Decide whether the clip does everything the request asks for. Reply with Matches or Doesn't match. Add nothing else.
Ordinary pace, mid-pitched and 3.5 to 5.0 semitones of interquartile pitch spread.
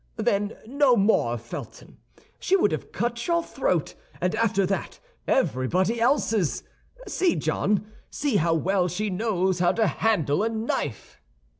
Doesn't match